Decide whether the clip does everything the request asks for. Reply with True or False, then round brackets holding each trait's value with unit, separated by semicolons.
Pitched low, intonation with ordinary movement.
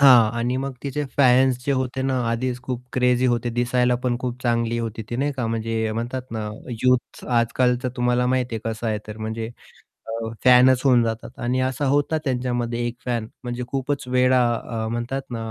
False (125 Hz; 1.6 semitones)